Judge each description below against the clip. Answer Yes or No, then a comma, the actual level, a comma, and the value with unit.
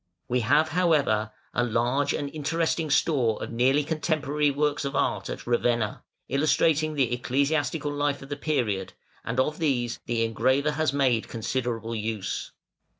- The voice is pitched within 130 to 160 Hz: Yes, medium, 140 Hz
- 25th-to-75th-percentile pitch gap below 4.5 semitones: Yes, average, 3.8 semitones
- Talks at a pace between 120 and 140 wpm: No, average, 150 wpm